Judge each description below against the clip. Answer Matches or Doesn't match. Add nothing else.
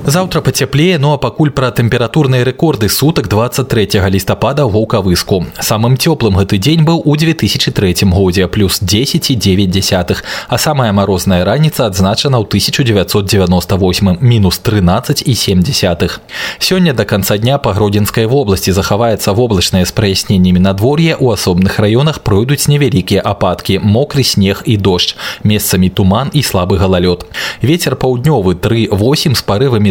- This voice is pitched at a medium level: Doesn't match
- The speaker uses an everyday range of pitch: Doesn't match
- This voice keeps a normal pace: Matches